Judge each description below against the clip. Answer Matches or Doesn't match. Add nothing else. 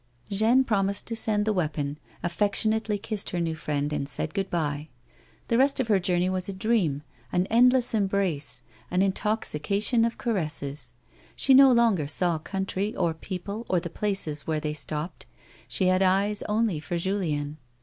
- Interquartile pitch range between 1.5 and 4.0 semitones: Doesn't match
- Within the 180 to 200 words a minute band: Doesn't match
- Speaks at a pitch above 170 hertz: Matches